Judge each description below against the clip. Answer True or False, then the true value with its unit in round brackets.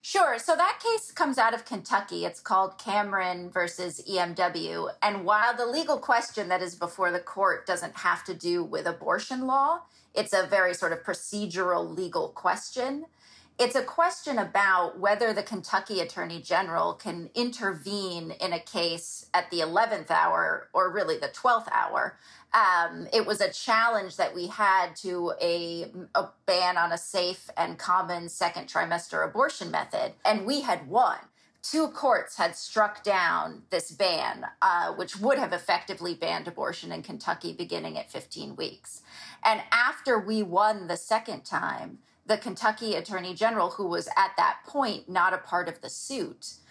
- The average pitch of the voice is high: True (200 Hz)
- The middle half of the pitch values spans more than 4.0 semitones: True (5.1 semitones)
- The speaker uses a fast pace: False (165 wpm)